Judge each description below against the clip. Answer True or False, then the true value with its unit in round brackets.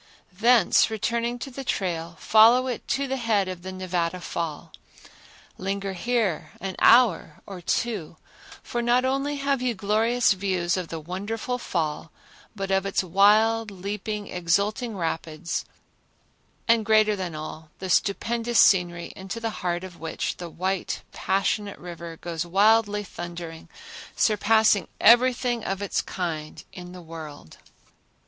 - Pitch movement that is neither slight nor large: True (4.6 semitones)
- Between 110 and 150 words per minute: True (140 wpm)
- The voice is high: True (195 Hz)